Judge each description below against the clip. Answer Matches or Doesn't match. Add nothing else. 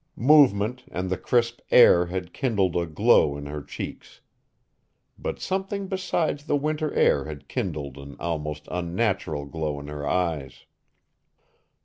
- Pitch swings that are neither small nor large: Doesn't match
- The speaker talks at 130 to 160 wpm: Matches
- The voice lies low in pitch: Matches